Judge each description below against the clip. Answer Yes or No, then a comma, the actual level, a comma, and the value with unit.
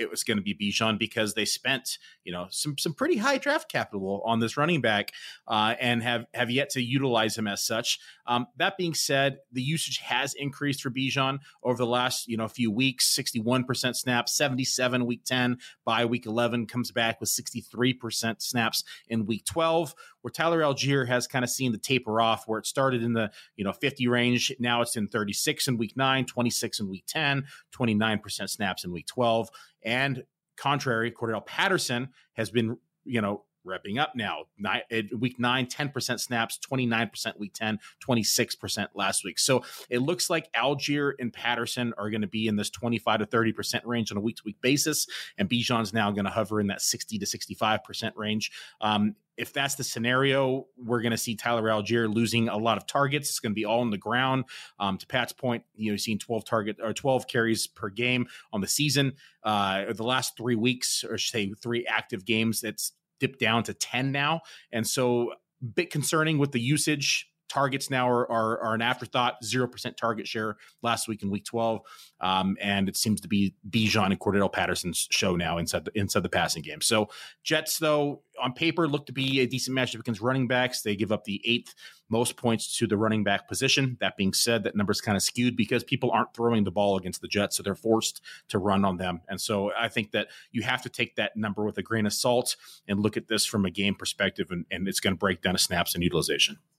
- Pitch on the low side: Yes, low, 120 Hz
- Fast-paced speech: Yes, fast, 210 wpm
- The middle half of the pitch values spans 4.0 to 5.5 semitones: No, average, 3.2 semitones